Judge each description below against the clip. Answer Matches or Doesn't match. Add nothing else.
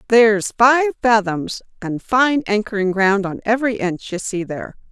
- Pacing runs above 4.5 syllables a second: Matches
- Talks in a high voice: Matches